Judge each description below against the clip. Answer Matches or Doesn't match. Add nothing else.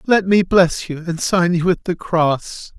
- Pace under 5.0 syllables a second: Matches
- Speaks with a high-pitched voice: Doesn't match